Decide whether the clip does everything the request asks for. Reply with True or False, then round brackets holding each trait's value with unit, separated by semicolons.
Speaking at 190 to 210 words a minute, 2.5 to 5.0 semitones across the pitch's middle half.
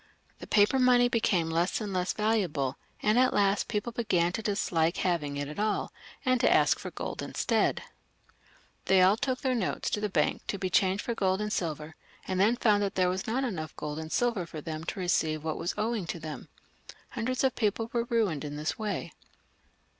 False (205 wpm; 5.4 semitones)